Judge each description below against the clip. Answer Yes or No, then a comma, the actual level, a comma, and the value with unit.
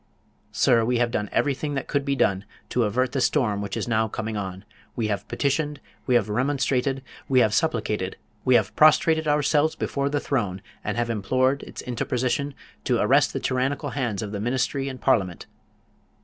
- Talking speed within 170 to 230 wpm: Yes, average, 180 wpm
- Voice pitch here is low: Yes, low, 125 Hz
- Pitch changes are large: No, average, 4.5 semitones